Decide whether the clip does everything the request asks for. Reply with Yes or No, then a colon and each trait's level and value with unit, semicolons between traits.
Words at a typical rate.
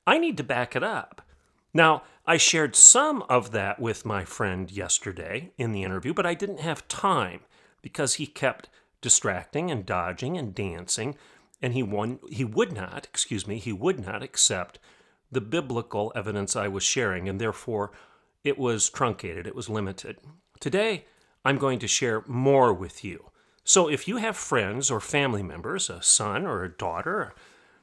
Yes: average, 175 wpm